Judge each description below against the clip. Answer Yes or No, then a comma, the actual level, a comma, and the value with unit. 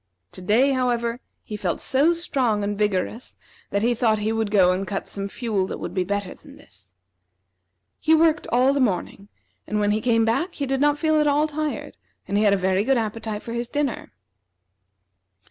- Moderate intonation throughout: Yes, average, 5.0 semitones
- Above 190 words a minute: Yes, average, 200 wpm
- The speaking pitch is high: Yes, high, 225 Hz